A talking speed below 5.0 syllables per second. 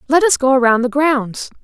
No: 5.2 syllables/s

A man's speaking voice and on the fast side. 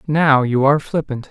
No: male; average, 185 wpm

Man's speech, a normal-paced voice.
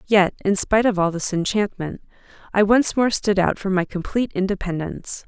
No: female; average, 180 wpm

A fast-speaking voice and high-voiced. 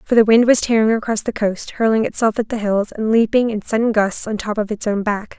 Yes: fast, 265 wpm; high, 220 Hz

